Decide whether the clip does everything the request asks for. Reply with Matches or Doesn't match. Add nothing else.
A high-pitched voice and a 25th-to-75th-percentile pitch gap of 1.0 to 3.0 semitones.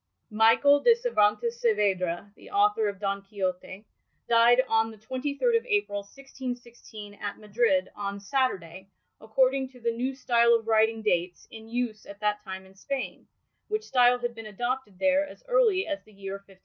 Doesn't match